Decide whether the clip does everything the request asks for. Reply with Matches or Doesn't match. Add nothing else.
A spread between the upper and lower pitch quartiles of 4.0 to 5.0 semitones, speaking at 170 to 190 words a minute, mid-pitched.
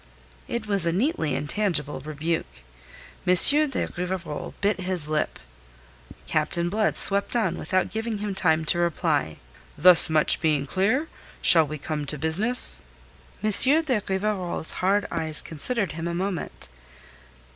Doesn't match